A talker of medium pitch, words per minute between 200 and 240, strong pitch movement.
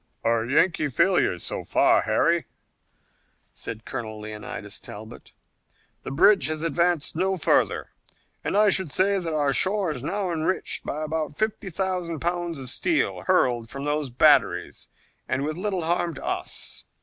No: medium, 160 Hz; average, 150 wpm; wide, 5.7 semitones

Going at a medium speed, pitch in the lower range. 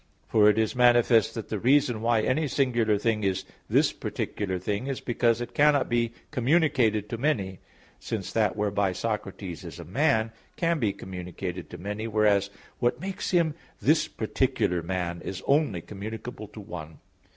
Yes: average, 160 wpm; low, 110 Hz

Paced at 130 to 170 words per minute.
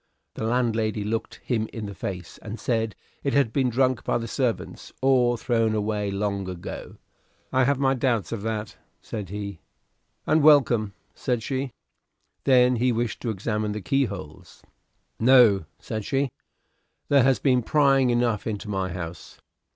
Yes: average, 155 wpm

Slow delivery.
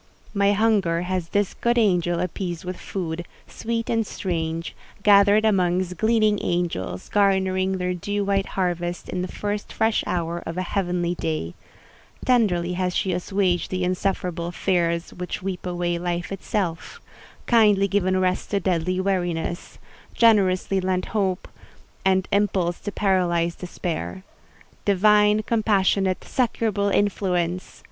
Yes: slow, 125 wpm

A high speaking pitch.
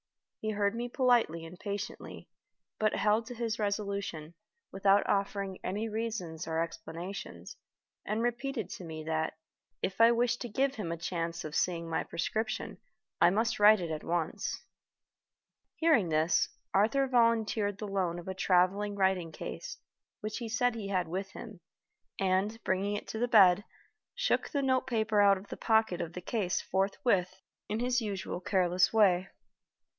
Yes: high, 200 Hz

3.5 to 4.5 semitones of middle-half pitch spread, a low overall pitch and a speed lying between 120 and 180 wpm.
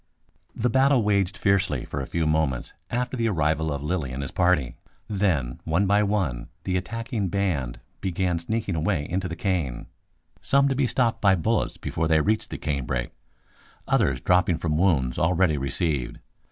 No: average, 5.3 semitones; very low, 90 Hz; average, 165 wpm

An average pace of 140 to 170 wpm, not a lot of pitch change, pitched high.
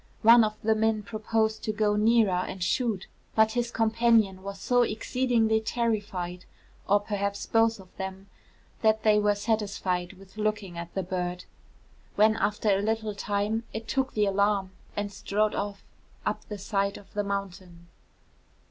Yes: average, 155 wpm; narrow, 2.1 semitones; high, 210 Hz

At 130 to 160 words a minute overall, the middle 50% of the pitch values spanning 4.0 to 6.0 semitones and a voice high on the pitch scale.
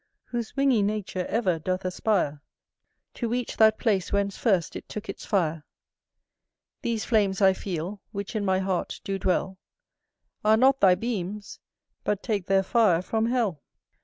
No: average, 155 wpm; average, 3.1 semitones; high, 200 Hz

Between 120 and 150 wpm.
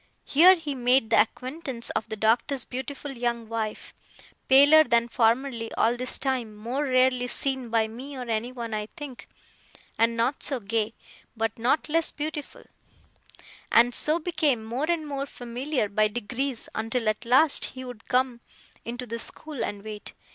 No: average, 160 wpm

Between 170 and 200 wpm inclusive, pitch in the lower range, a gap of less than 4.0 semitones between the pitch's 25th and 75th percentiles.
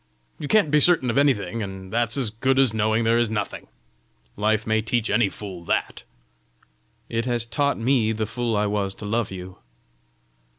Yes: average, 180 wpm; low, 110 Hz; average, 2.7 semitones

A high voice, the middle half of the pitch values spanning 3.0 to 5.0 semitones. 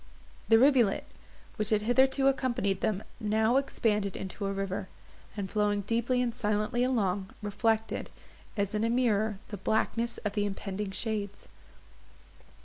No: high, 215 Hz; narrow, 2.6 semitones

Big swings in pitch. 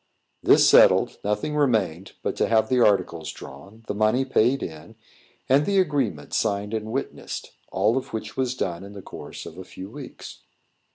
No: average, 5.0 semitones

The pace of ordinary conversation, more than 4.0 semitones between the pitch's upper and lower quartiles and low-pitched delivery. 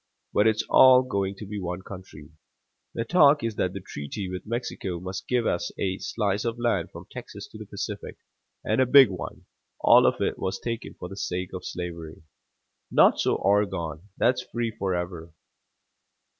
Yes: average, 175 wpm; average, 4.4 semitones; low, 100 Hz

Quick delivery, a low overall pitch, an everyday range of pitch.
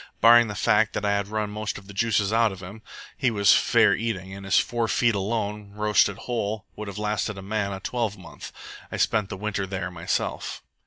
No: fast, 210 wpm; low, 105 Hz; narrow, 1.9 semitones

